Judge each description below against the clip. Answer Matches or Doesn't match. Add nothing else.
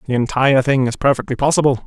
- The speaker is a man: Matches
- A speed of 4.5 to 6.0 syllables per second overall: Doesn't match